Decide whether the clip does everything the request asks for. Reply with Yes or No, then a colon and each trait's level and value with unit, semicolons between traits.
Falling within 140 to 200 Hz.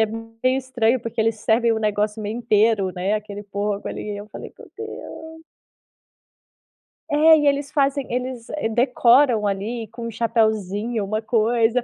No: high, 225 Hz